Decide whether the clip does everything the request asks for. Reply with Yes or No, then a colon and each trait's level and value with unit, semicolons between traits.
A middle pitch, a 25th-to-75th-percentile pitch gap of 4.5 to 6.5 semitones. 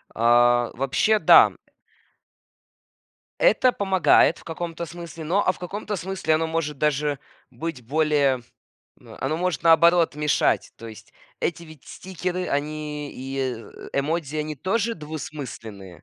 No: medium, 155 Hz; average, 4.1 semitones